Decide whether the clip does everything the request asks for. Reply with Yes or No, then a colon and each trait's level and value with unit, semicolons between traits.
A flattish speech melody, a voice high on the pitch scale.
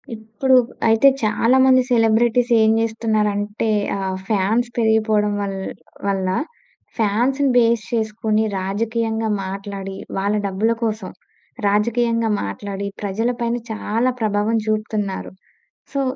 Yes: narrow, 2.1 semitones; high, 220 Hz